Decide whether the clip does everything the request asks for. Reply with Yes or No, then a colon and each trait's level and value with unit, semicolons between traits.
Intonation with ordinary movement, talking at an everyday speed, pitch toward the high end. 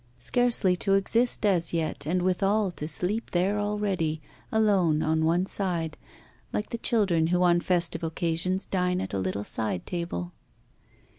No: average, 3.5 semitones; average, 150 wpm; medium, 180 Hz